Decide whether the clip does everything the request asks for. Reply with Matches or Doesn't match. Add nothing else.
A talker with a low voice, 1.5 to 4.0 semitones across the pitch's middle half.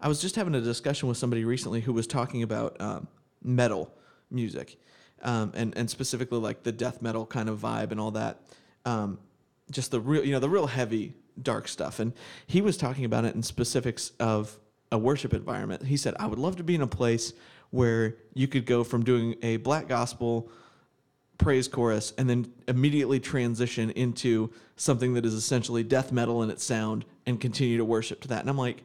Matches